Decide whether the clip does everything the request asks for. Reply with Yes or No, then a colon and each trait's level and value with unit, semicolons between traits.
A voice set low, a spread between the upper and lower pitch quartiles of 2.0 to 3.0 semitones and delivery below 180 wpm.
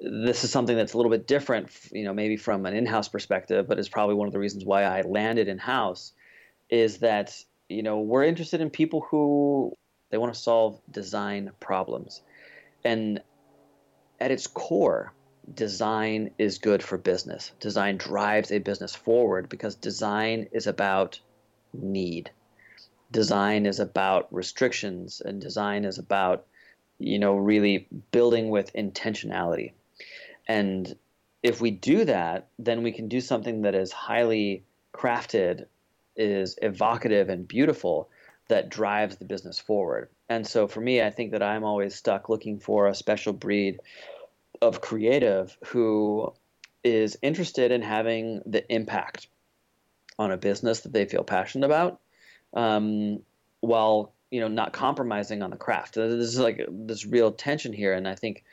Yes: low, 105 Hz; narrow, 2.4 semitones; average, 155 wpm